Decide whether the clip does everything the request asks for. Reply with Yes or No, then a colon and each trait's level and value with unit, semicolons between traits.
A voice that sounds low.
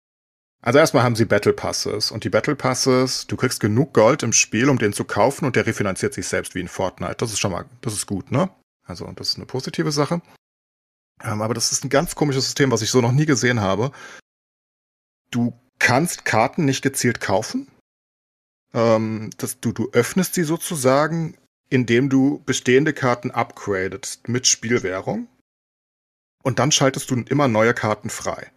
Yes: low, 130 Hz